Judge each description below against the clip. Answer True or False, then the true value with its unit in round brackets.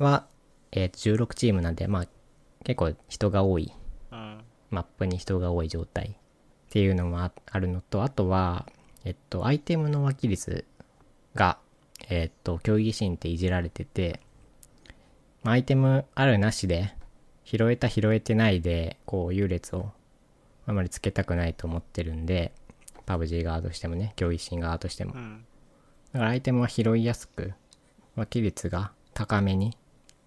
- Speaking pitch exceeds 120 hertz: False (95 Hz)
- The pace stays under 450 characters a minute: True (290 characters per minute)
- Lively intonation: False (4.7 semitones)